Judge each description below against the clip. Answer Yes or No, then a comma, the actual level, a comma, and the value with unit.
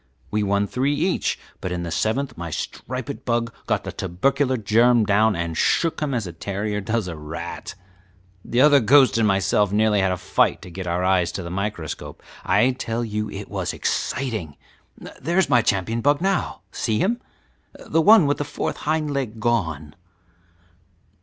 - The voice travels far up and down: Yes, wide, 6.0 semitones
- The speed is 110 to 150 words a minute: No, average, 180 wpm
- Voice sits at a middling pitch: No, low, 110 Hz